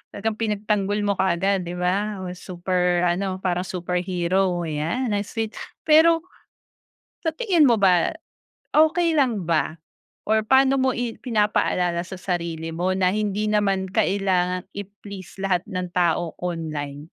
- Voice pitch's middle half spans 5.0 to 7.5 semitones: No, average, 3.2 semitones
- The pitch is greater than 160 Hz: Yes, high, 190 Hz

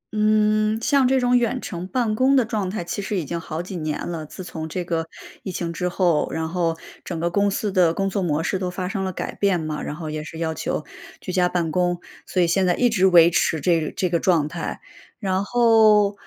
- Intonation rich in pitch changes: No, average, 4.0 semitones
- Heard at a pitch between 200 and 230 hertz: No, medium, 185 Hz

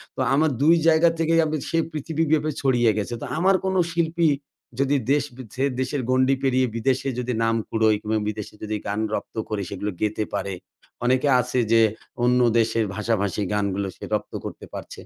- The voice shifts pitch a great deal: Yes, wide, 5.8 semitones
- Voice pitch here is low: Yes, low, 130 Hz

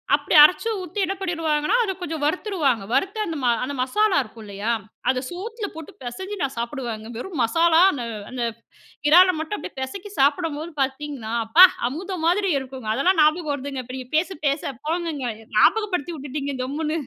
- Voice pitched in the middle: No, very high, 305 Hz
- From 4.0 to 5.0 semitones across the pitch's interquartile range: No, wide, 5.5 semitones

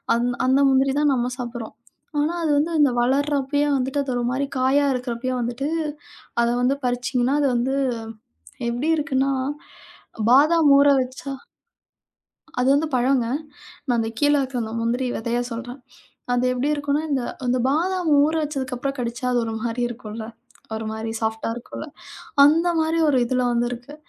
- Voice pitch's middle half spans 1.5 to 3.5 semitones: Yes, average, 3.0 semitones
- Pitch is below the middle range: No, very high, 260 Hz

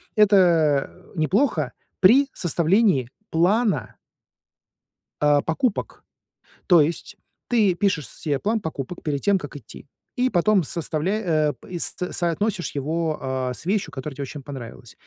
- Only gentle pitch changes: No, wide, 5.6 semitones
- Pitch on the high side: No, medium, 170 Hz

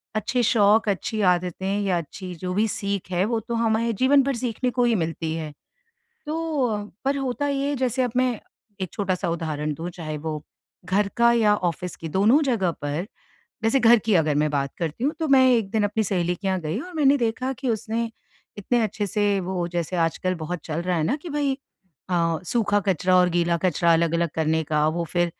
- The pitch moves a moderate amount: No, wide, 5.7 semitones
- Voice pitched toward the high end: Yes, high, 195 Hz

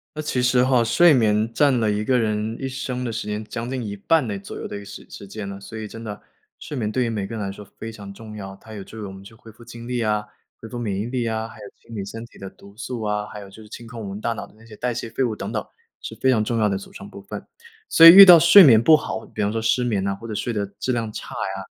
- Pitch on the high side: No, low, 110 Hz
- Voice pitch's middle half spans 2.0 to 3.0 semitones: Yes, average, 2.7 semitones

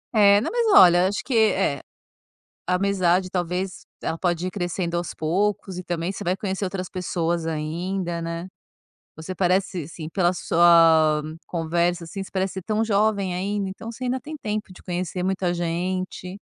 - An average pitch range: No, narrow, 2.3 semitones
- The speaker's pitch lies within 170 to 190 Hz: Yes, medium, 185 Hz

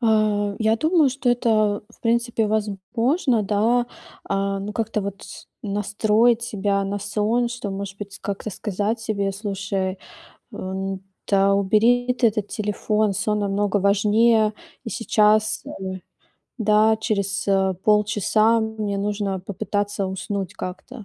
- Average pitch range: No, narrow, 1.9 semitones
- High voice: Yes, high, 210 Hz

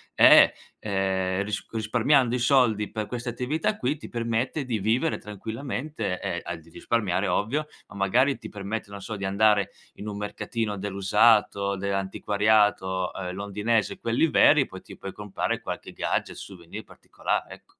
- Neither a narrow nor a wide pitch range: Yes, average, 3.2 semitones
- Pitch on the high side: No, low, 105 Hz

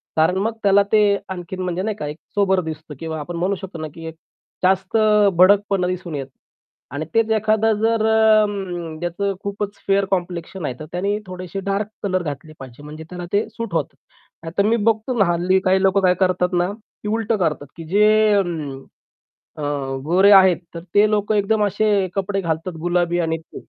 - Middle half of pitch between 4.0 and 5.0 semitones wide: No, average, 3.2 semitones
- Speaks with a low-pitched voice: No, medium, 185 Hz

